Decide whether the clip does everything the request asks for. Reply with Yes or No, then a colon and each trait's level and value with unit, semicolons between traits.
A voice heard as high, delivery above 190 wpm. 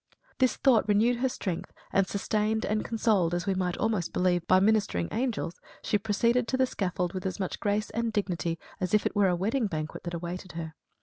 Yes: high, 200 Hz; average, 200 wpm